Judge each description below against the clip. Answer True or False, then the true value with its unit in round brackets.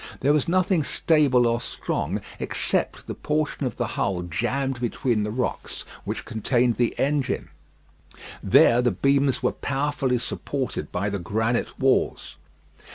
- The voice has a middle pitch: False (125 Hz)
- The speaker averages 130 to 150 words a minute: True (140 wpm)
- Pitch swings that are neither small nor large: True (3.5 semitones)